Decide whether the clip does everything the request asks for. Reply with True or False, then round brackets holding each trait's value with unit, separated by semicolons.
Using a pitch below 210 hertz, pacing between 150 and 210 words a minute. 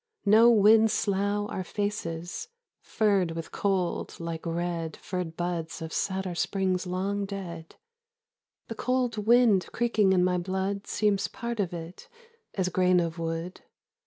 False (190 Hz; 135 wpm)